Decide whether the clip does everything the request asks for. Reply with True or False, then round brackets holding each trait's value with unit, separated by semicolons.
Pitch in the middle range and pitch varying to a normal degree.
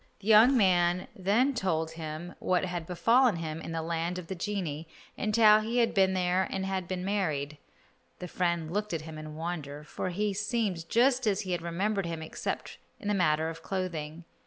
True (180 Hz; 4.0 semitones)